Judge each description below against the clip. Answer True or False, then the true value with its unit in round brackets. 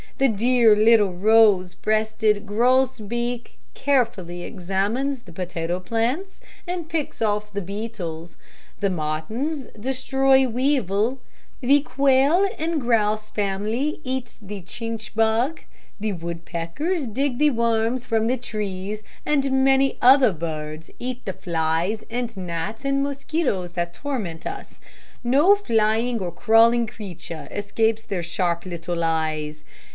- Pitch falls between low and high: False (220 Hz)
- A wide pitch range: True (5.9 semitones)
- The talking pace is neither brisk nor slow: False (125 wpm)